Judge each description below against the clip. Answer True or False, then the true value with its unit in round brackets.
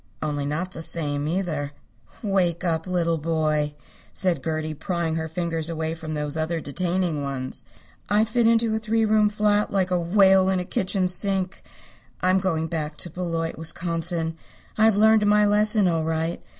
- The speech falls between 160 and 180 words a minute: True (165 wpm)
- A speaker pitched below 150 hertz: False (170 Hz)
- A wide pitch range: False (3.3 semitones)